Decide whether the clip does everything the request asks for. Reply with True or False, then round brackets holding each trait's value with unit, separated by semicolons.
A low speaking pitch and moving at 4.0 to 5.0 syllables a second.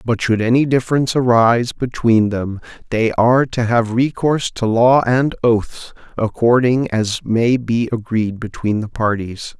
True (115 Hz; 4.4 syllables/s)